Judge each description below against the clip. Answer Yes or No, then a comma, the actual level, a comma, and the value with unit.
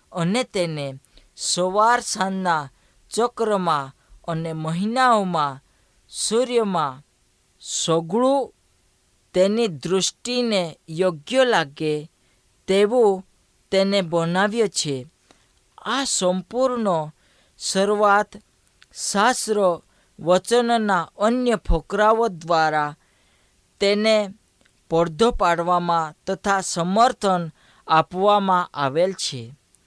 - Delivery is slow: Yes, slow, 65 wpm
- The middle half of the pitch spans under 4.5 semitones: No, average, 5.1 semitones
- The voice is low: No, medium, 185 Hz